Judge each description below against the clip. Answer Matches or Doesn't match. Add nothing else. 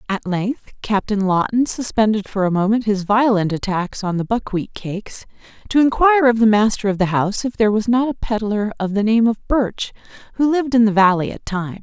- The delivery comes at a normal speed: Doesn't match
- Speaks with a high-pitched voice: Matches